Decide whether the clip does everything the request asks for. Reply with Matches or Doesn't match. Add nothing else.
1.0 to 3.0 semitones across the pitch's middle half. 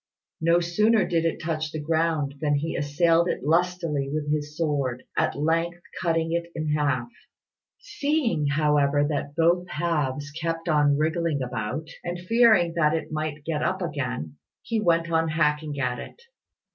Matches